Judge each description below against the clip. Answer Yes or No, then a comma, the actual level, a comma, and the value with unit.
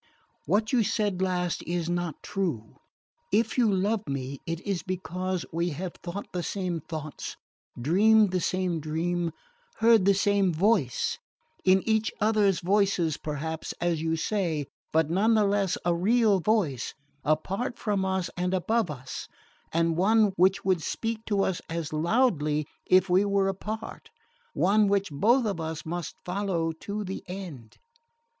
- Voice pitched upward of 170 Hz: Yes, medium, 185 Hz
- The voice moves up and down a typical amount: Yes, average, 3.7 semitones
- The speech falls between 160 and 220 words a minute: No, average, 150 wpm